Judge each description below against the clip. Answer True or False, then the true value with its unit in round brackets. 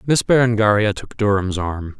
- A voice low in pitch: True (105 Hz)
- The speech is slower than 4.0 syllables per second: False (4.9 syllables/s)